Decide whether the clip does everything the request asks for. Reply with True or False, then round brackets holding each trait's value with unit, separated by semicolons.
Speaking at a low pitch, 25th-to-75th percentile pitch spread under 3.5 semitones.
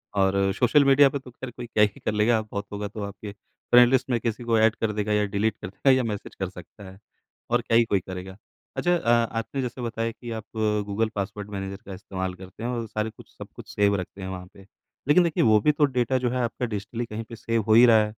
True (110 Hz; 3.0 semitones)